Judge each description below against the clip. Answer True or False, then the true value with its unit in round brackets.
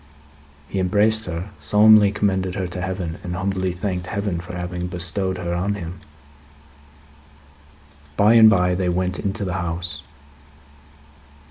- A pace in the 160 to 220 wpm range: False (135 wpm)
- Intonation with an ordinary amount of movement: False (2.2 semitones)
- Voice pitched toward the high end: False (95 Hz)